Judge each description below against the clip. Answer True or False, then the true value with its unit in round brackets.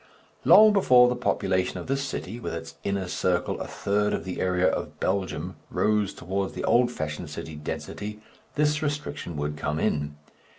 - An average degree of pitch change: False (5.7 semitones)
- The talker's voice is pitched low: True (100 Hz)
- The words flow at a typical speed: True (170 wpm)